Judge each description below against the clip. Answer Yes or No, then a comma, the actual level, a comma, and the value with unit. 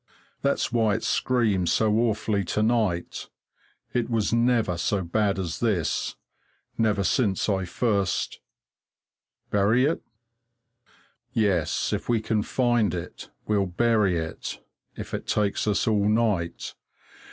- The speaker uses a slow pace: Yes, slow, 125 wpm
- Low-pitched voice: Yes, low, 105 Hz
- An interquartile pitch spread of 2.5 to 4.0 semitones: Yes, average, 3.3 semitones